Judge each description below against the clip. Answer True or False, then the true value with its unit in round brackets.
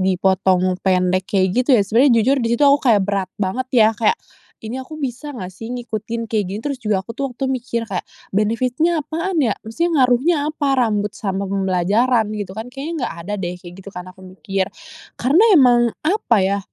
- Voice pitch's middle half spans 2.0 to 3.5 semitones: False (5.4 semitones)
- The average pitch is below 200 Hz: False (225 Hz)